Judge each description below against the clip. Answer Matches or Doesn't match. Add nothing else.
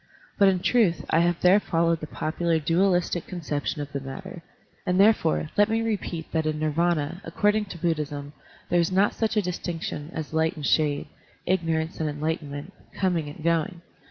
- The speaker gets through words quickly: Doesn't match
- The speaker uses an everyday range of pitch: Matches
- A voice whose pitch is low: Doesn't match